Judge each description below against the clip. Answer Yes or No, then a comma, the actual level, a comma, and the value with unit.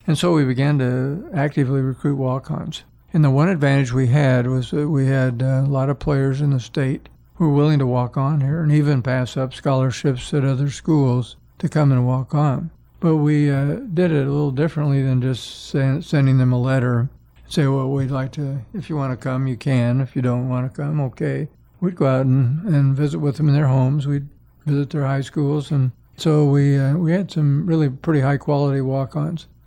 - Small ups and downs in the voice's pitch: Yes, narrow, 2.2 semitones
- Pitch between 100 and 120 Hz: No, medium, 140 Hz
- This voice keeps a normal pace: No, fast, 220 wpm